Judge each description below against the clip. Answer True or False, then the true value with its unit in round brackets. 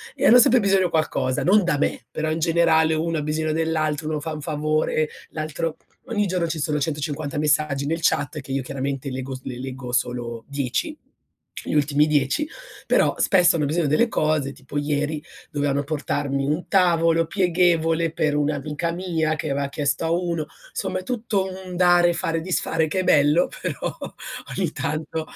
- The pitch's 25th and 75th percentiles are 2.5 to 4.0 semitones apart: True (2.8 semitones)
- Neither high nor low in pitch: True (155 Hz)